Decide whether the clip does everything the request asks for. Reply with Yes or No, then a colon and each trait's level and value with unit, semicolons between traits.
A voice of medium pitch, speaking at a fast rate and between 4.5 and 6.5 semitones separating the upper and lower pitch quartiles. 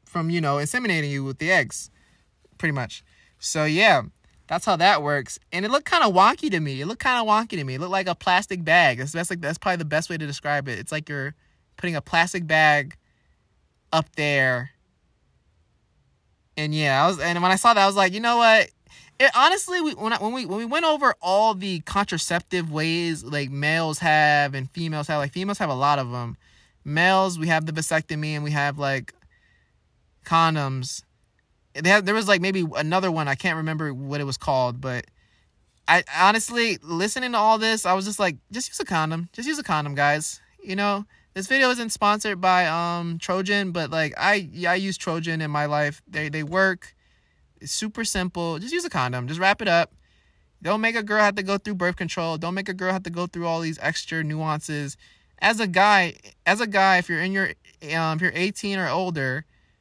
Yes: medium, 170 Hz; fast, 215 wpm; average, 4.9 semitones